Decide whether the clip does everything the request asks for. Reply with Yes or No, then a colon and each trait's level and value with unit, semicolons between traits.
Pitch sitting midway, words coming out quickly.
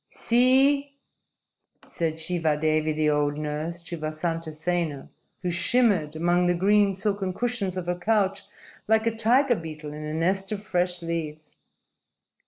No: medium, 175 Hz; average, 140 wpm